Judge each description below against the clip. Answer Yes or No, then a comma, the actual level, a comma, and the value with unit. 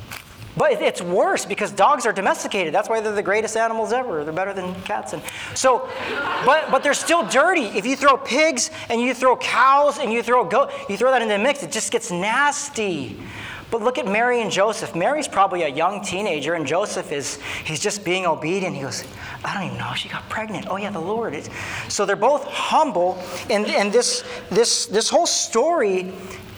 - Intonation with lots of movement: Yes, wide, 7.0 semitones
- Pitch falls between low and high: No, high, 225 Hz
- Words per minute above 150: Yes, fast, 205 wpm